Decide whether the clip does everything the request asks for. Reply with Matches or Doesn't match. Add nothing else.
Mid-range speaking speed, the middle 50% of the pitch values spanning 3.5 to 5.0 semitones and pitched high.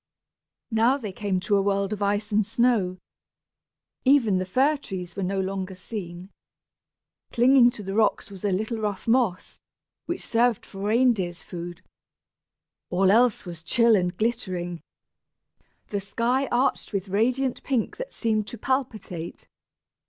Matches